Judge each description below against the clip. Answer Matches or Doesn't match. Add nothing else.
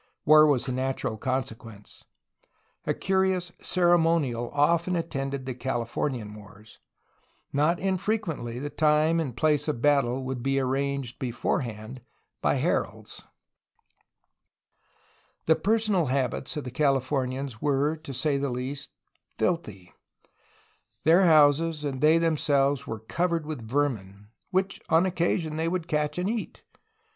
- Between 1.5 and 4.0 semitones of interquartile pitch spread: Doesn't match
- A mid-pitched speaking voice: Matches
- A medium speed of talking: Doesn't match